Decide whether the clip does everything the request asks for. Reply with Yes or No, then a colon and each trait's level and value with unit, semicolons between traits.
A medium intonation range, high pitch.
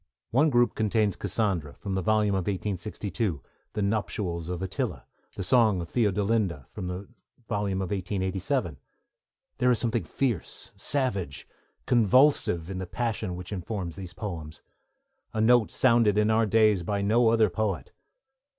No: average, 3.5 semitones; low, 105 Hz